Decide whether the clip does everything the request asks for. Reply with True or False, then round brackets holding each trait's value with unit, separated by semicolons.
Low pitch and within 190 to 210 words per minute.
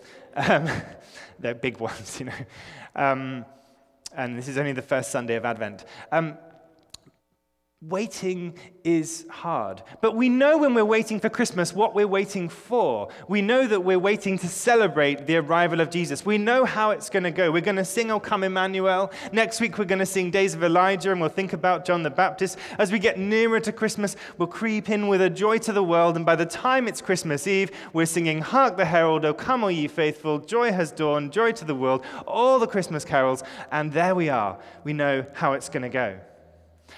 False (180 Hz; 205 wpm)